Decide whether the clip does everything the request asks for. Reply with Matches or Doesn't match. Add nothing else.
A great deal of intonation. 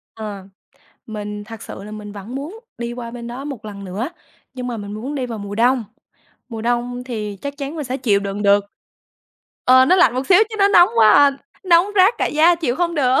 Doesn't match